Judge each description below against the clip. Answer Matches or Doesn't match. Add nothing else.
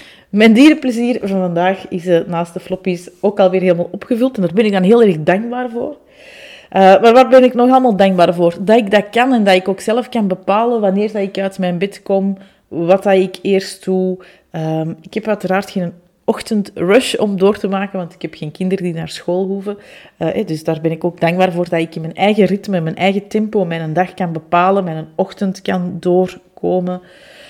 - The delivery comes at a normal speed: Doesn't match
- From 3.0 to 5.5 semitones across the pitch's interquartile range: Doesn't match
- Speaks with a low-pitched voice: Doesn't match